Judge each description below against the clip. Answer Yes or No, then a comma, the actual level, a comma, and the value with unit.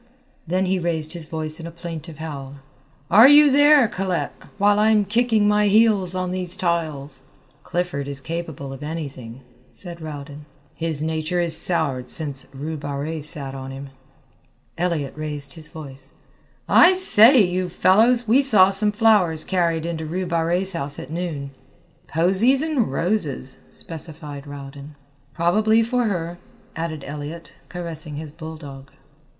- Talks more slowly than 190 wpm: Yes, average, 145 wpm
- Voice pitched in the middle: Yes, medium, 165 Hz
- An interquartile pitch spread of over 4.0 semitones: Yes, average, 4.4 semitones